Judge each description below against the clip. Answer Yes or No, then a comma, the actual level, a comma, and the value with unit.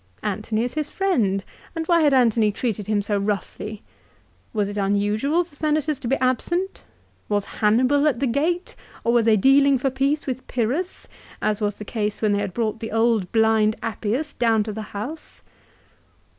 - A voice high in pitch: Yes, high, 230 Hz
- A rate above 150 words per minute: Yes, average, 175 wpm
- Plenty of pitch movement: No, average, 5.0 semitones